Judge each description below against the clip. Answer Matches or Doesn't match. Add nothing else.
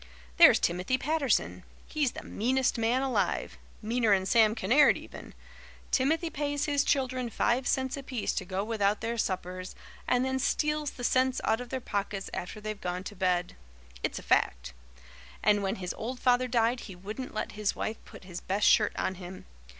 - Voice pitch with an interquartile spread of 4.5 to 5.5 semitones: Matches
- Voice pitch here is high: Matches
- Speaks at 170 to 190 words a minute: Matches